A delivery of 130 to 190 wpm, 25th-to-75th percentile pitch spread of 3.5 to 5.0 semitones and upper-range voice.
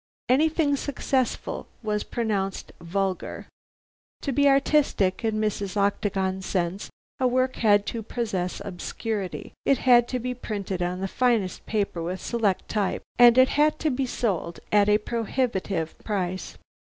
Yes: average, 140 wpm; average, 4.7 semitones; high, 210 Hz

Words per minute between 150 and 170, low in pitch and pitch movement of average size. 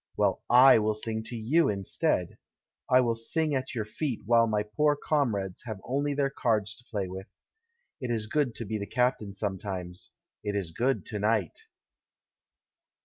No: average, 180 wpm; low, 110 Hz; average, 3.9 semitones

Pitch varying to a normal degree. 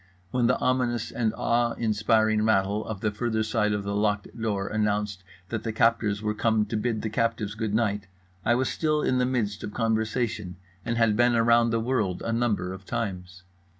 No: narrow, 2.1 semitones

